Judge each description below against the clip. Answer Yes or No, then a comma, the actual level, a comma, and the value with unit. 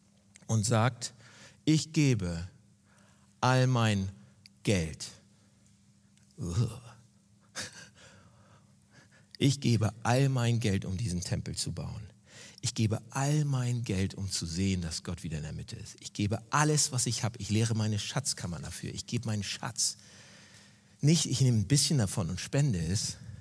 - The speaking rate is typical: Yes, average, 145 wpm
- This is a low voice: Yes, low, 115 Hz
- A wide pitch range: No, average, 4.1 semitones